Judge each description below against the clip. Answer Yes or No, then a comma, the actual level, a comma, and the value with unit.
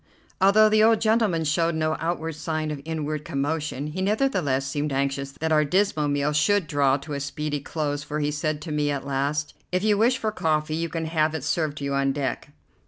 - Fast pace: Yes, fast, 215 wpm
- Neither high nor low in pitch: Yes, medium, 155 Hz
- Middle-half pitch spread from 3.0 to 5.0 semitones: No, narrow, 2.5 semitones